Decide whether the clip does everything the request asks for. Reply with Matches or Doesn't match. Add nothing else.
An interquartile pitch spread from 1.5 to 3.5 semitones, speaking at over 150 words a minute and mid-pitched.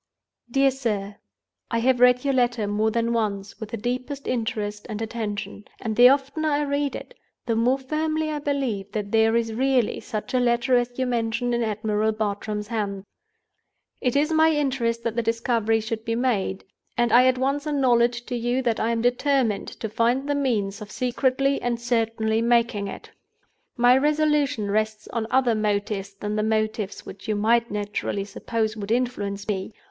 Doesn't match